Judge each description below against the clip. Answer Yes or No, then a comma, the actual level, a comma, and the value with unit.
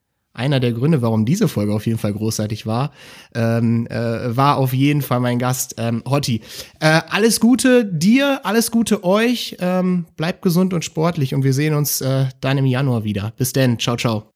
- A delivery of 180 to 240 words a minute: Yes, fast, 190 wpm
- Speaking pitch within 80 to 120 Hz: No, low, 135 Hz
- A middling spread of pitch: No, wide, 7.0 semitones